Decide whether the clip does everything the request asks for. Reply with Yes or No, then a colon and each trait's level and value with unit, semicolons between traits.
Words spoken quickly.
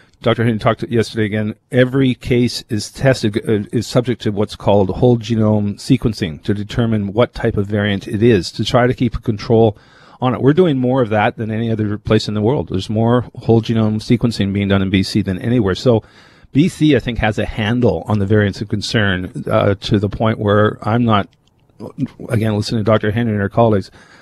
Yes: fast, 210 wpm